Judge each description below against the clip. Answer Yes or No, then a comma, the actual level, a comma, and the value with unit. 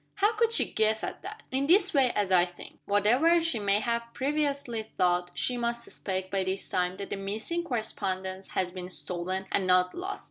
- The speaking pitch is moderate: No, high, 215 Hz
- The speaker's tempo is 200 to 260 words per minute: Yes, fast, 205 wpm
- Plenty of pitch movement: Yes, wide, 7.0 semitones